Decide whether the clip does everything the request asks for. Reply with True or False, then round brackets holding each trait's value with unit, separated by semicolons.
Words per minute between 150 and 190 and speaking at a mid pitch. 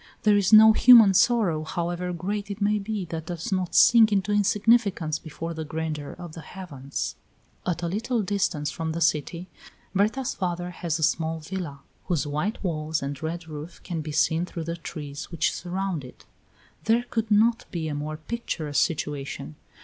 True (175 wpm; 175 Hz)